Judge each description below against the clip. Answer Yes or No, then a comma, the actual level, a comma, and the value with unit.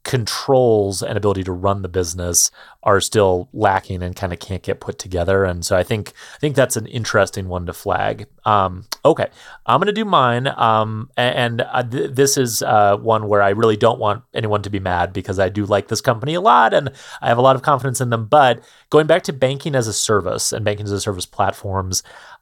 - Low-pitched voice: Yes, low, 105 Hz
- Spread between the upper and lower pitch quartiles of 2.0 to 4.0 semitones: No, average, 4.6 semitones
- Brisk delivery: Yes, fast, 225 wpm